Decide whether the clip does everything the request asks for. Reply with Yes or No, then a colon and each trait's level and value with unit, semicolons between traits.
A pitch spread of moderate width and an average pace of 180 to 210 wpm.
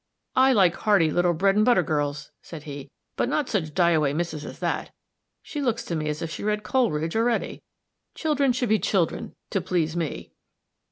No: wide, 6.1 semitones; average, 190 wpm